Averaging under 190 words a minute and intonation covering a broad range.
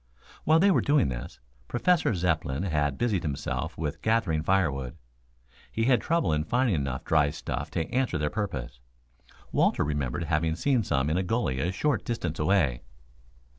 Yes: average, 165 wpm; wide, 7.7 semitones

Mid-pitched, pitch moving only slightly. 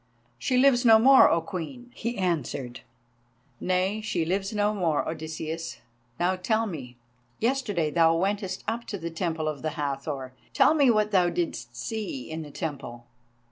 No: medium, 175 Hz; average, 5.3 semitones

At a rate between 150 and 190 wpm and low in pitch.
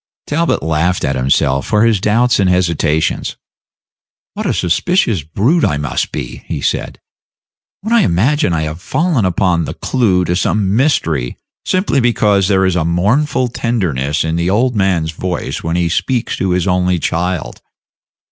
Yes: average, 160 wpm; very low, 90 Hz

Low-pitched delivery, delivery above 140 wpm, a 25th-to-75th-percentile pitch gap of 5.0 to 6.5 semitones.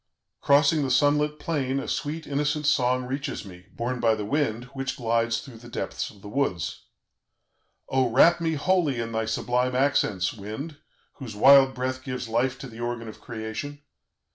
No: low, 130 Hz; average, 175 wpm; average, 3.7 semitones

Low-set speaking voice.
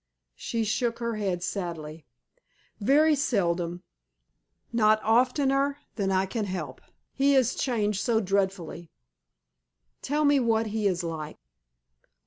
No: high, 215 Hz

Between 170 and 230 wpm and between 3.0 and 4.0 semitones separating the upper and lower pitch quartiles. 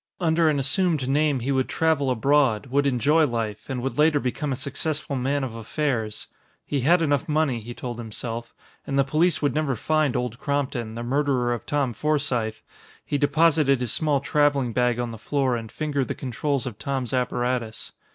Yes: average, 185 wpm; average, 3.3 semitones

